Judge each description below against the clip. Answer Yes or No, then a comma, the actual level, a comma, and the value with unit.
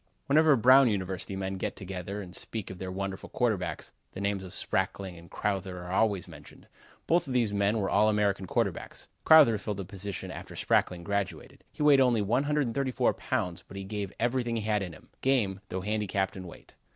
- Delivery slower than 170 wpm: No, average, 190 wpm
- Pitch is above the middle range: No, low, 100 Hz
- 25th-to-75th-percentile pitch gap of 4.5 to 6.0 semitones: No, average, 3.6 semitones